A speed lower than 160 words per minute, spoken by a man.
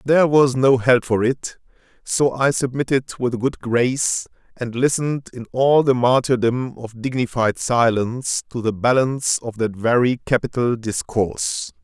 Yes: average, 150 wpm; male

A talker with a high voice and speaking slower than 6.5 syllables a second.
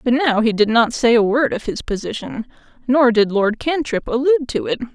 Yes: high, 240 Hz; 5.4 syllables/s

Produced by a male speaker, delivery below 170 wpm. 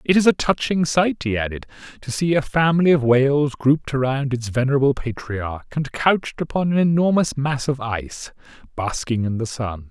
No: male; average, 180 wpm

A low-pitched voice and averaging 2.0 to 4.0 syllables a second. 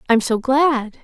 No: very high, 255 Hz; 3.8 syllables/s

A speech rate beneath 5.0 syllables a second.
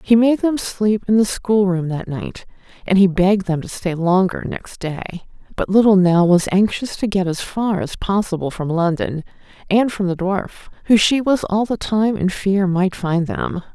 Yes: 4.6 syllables/s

